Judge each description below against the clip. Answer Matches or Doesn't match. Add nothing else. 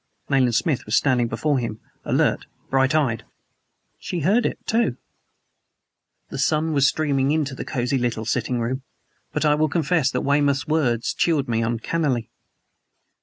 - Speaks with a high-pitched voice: Doesn't match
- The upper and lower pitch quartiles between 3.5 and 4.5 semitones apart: Matches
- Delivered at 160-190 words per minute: Doesn't match